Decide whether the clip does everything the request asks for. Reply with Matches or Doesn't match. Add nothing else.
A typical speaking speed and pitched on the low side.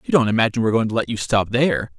Doesn't match